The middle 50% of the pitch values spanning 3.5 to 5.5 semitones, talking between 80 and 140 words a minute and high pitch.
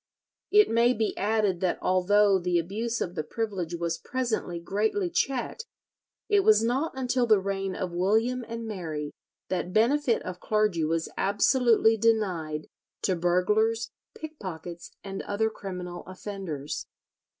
Yes: average, 4.5 semitones; slow, 135 wpm; high, 205 Hz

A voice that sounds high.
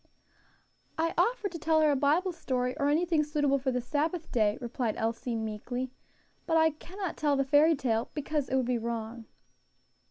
Yes: very high, 280 Hz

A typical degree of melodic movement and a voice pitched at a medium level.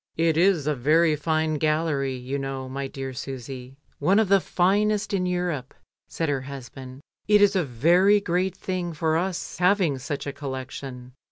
Yes: average, 5.0 semitones; medium, 155 Hz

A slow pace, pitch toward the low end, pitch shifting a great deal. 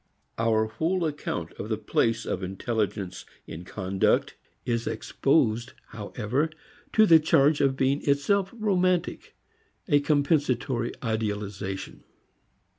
Yes: slow, 110 wpm; low, 120 Hz; wide, 5.9 semitones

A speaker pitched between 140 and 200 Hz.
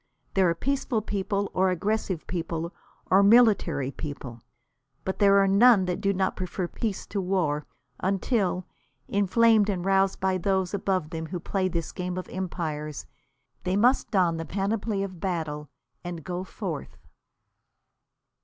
Yes: medium, 185 Hz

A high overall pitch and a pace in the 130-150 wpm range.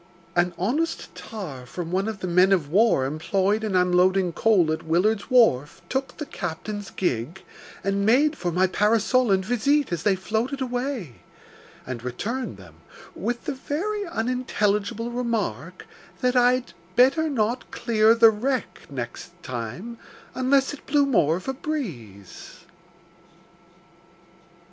Yes: high, 210 Hz; slow, 135 wpm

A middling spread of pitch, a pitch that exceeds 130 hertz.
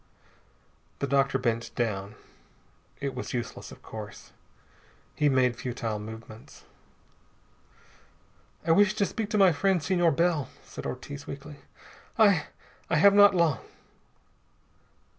No: wide, 6.7 semitones; medium, 140 Hz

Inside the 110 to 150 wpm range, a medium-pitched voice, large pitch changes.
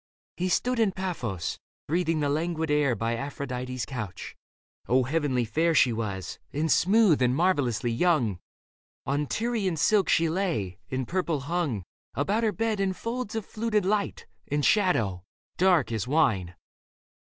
Yes: average, 145 wpm; medium, 155 Hz; wide, 7.1 semitones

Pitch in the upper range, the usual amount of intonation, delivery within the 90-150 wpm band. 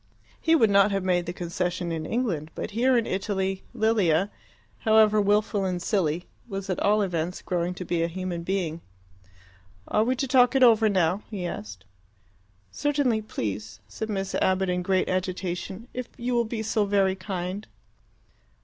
No: high, 195 Hz; average, 3.6 semitones; average, 165 wpm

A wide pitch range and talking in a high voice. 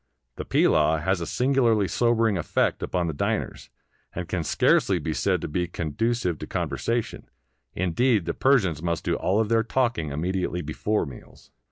No: wide, 5.9 semitones; very low, 90 Hz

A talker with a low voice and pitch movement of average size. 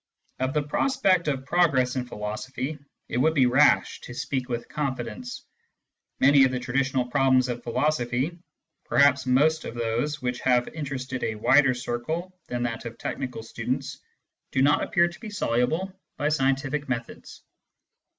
Yes: low, 130 Hz; average, 3.3 semitones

